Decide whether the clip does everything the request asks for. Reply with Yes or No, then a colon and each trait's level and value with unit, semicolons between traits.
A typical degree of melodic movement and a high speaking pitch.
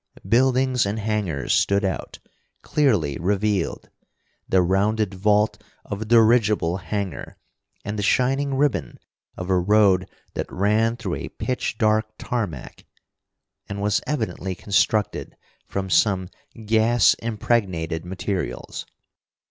No: average, 3.1 semitones; low, 105 Hz